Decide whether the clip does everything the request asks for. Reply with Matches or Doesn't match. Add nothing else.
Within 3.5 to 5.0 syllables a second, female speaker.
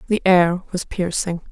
Matches